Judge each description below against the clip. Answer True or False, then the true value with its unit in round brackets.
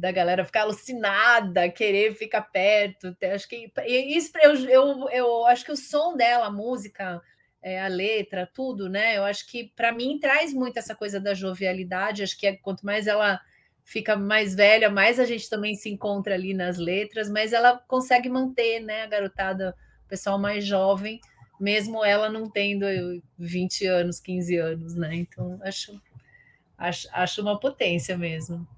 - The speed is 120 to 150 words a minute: False (165 wpm)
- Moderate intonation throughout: True (3.7 semitones)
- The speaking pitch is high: True (205 Hz)